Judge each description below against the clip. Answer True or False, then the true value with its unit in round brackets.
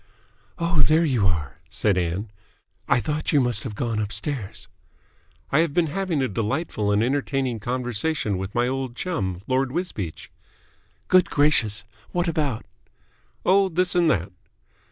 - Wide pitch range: True (7.2 semitones)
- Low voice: True (130 Hz)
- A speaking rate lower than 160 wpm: True (145 wpm)